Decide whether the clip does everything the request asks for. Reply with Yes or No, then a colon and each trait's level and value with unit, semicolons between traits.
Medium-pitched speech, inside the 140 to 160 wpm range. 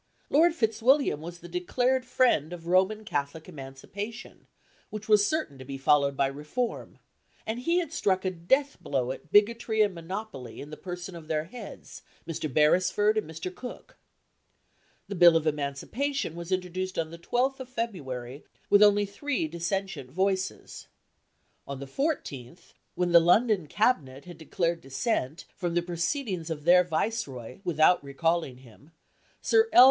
Yes: medium, 175 Hz; average, 155 wpm